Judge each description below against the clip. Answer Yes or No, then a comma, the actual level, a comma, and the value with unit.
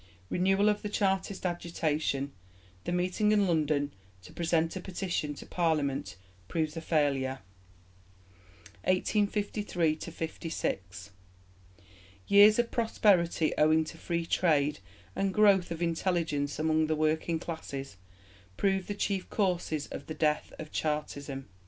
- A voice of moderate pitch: Yes, medium, 165 Hz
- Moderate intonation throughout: Yes, average, 3.9 semitones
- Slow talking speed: Yes, slow, 120 wpm